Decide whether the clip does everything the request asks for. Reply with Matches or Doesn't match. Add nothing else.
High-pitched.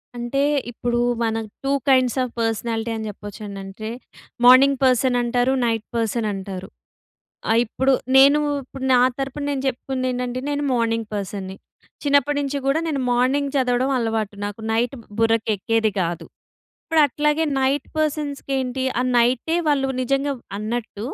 Matches